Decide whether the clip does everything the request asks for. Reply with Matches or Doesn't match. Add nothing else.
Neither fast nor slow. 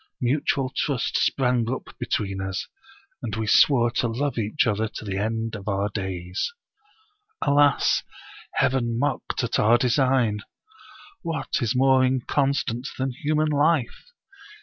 Doesn't match